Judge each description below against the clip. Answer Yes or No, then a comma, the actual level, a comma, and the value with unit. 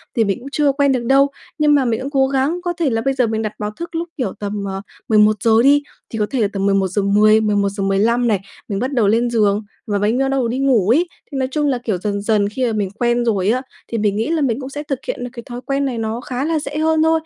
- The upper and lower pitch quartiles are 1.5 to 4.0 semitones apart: No, average, 4.6 semitones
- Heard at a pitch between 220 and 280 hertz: Yes, high, 235 Hz